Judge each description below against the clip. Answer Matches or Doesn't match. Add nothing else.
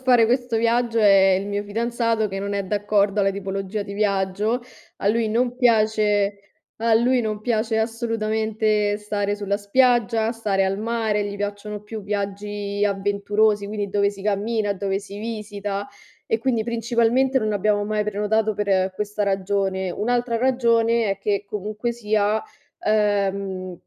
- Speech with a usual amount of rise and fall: Doesn't match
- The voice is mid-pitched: Doesn't match